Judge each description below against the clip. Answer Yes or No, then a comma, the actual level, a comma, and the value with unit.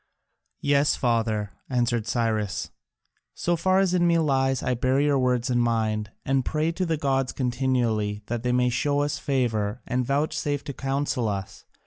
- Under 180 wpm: Yes, average, 165 wpm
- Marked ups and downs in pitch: No, average, 3.7 semitones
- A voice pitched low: Yes, low, 125 Hz